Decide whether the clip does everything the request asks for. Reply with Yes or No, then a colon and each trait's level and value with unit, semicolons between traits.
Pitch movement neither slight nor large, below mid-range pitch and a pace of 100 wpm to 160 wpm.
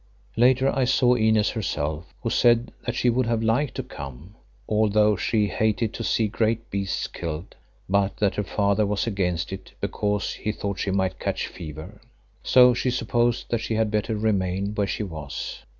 No: average, 3.2 semitones; low, 105 Hz; average, 180 wpm